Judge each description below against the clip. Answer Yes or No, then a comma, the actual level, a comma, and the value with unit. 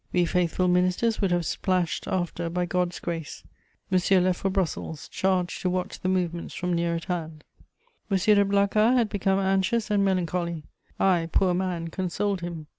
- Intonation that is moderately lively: No, narrow, 1.9 semitones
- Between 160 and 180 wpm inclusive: Yes, average, 170 wpm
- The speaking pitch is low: No, medium, 180 Hz